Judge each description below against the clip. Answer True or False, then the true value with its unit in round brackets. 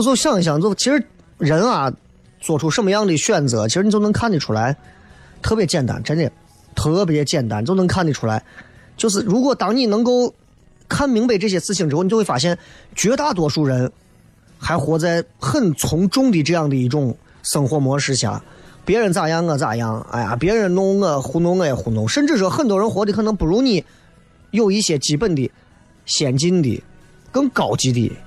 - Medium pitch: True (165 Hz)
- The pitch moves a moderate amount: False (7.5 semitones)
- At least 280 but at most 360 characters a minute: True (285 characters per minute)